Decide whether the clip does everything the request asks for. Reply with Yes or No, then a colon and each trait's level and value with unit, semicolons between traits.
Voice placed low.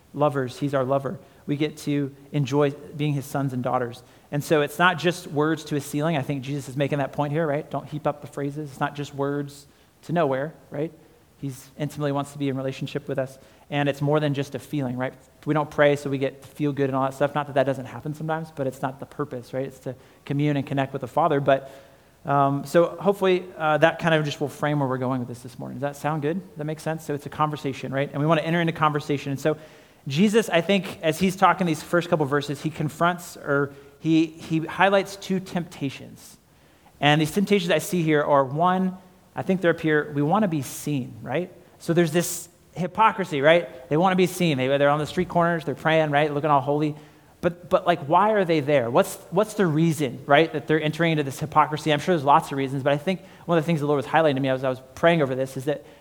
No: medium, 150 Hz